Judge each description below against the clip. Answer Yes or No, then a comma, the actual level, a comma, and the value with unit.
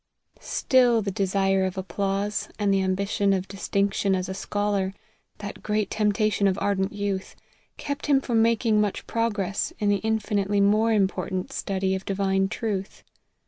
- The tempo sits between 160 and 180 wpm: No, average, 150 wpm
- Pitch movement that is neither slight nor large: No, narrow, 1.6 semitones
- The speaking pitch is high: Yes, high, 200 Hz